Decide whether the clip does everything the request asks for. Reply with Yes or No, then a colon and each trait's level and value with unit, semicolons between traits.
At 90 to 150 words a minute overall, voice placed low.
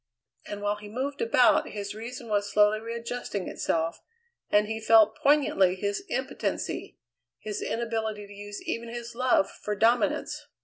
No: average, 145 wpm; high, 215 Hz